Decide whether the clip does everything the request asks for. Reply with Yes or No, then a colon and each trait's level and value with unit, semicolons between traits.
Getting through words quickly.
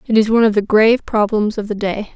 Yes: fast, 280 wpm